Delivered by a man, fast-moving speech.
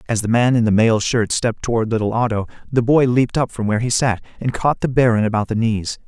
Yes: male; fast, 255 wpm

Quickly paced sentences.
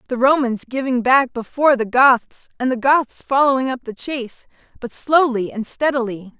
No: average, 170 wpm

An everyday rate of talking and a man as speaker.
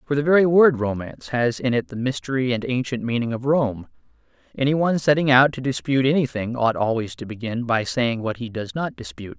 No: fast, 210 wpm; male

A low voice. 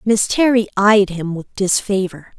No: high, 200 Hz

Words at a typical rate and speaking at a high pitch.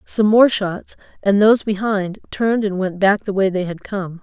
No: fast, 215 wpm; high, 200 Hz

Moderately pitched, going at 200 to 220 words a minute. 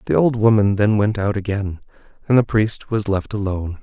No: low, 105 Hz; fast, 205 wpm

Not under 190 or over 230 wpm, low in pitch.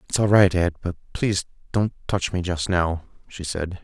Yes: fast, 205 wpm; very low, 90 Hz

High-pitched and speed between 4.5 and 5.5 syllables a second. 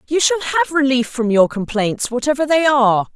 Yes: very high, 260 Hz; 5.0 syllables/s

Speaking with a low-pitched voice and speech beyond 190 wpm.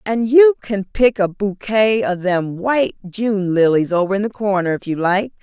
No: high, 205 Hz; average, 200 wpm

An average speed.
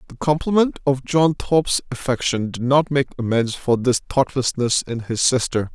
Yes: average, 165 wpm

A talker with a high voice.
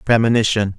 No: low, 110 Hz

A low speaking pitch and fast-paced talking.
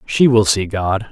Yes: low, 105 Hz; fast, 215 wpm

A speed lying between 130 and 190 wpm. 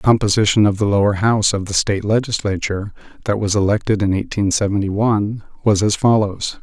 Yes: average, 180 wpm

